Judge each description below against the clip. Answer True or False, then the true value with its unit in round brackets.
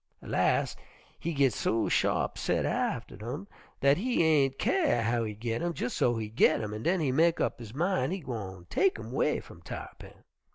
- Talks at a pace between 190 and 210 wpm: True (200 wpm)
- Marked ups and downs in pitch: True (6.8 semitones)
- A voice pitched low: True (130 Hz)